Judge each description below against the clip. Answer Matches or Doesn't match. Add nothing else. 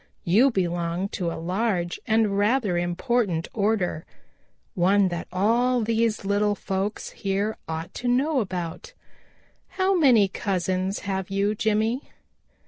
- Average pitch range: Matches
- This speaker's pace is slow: Matches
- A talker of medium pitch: Doesn't match